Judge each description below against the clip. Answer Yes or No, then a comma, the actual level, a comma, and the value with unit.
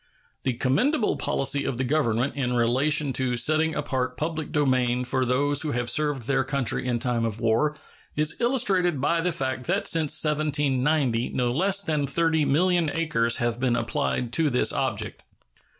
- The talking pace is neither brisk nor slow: Yes, average, 165 wpm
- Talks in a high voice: No, medium, 140 Hz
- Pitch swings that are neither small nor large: Yes, average, 3.9 semitones